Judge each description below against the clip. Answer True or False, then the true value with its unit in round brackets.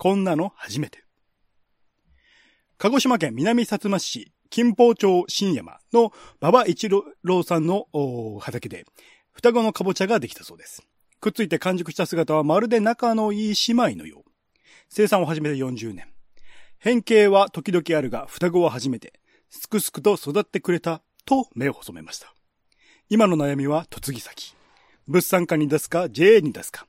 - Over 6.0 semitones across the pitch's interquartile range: False (5.5 semitones)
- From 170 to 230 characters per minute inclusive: False (290 characters per minute)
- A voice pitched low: False (185 Hz)